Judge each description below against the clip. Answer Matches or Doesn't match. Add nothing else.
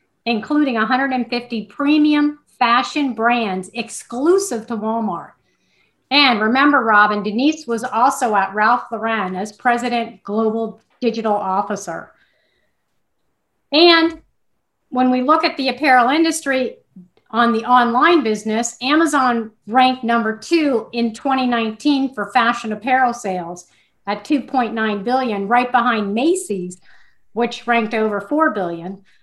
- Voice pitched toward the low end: Doesn't match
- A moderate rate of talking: Doesn't match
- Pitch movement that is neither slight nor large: Matches